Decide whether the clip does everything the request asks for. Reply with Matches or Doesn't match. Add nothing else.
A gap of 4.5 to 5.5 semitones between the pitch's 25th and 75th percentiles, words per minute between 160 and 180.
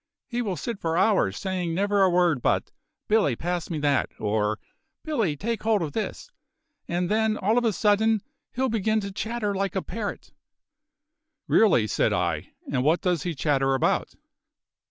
Matches